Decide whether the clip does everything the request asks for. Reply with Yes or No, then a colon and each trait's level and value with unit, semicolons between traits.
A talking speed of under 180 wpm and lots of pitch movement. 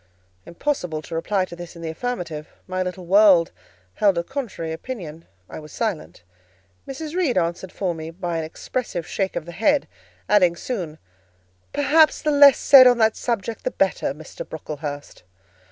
Yes: average, 165 wpm; wide, 6.9 semitones